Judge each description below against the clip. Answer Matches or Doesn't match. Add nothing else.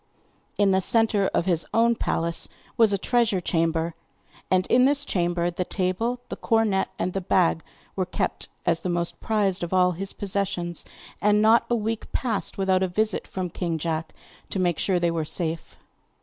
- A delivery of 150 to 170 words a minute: Doesn't match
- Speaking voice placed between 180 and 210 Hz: Matches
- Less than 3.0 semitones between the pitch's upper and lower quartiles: Doesn't match